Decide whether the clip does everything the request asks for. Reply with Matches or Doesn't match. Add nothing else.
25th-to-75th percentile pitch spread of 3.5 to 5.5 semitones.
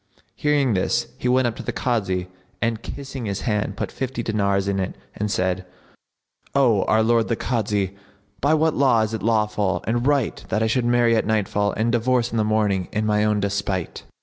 Doesn't match